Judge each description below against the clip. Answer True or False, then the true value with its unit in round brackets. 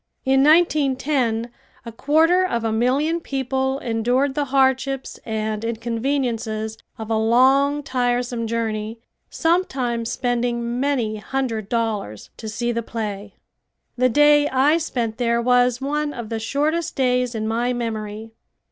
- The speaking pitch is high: True (245 Hz)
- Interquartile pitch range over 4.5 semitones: False (3.3 semitones)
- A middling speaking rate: False (130 wpm)